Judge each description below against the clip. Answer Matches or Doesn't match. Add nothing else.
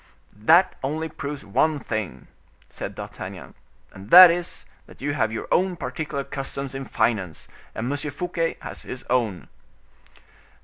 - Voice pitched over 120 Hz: Matches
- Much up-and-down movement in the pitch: Matches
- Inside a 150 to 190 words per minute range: Doesn't match